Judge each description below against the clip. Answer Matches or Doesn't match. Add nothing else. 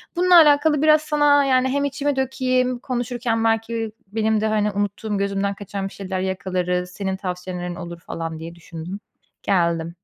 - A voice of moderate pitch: Doesn't match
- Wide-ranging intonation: Matches